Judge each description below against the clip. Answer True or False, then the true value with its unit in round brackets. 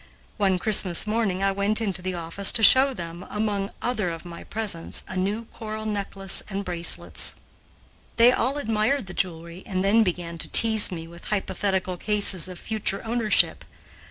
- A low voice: False (195 Hz)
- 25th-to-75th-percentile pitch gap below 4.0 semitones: True (3.1 semitones)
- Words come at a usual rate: True (165 wpm)